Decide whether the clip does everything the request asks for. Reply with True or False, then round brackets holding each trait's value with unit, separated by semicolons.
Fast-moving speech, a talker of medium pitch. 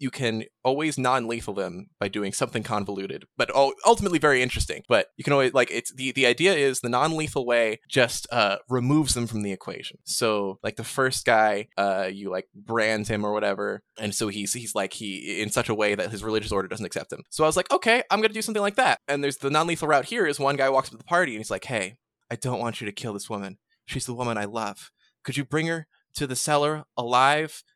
False (250 wpm; 120 Hz)